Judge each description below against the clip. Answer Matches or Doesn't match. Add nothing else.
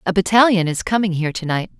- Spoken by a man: Doesn't match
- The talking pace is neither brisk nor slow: Doesn't match